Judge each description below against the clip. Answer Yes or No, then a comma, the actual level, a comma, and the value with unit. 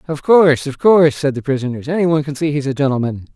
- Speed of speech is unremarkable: No, fast, 215 wpm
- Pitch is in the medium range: Yes, medium, 145 Hz